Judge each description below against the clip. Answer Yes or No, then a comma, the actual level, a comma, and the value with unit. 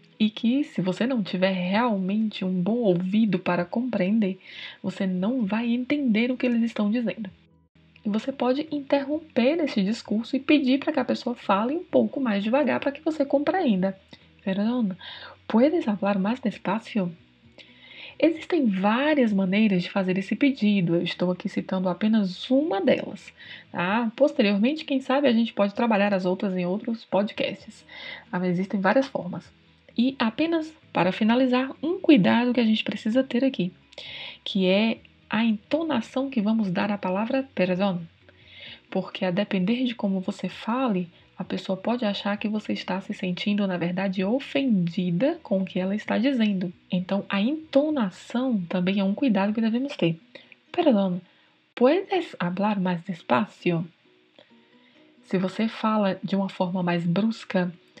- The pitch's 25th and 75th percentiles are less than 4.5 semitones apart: No, average, 5.3 semitones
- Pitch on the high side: Yes, high, 215 Hz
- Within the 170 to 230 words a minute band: No, average, 150 wpm